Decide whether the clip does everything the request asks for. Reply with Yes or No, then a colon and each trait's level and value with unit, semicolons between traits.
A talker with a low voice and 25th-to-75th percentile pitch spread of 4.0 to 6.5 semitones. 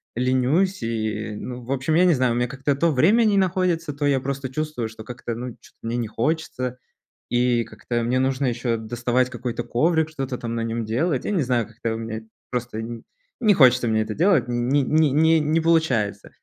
Yes: low, 125 Hz; average, 4.7 semitones